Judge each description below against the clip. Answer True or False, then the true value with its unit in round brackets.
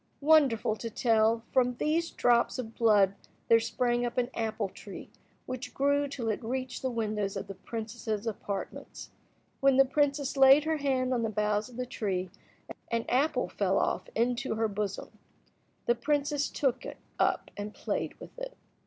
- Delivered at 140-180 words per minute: True (170 wpm)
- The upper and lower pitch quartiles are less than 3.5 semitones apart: False (3.8 semitones)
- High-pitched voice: True (240 Hz)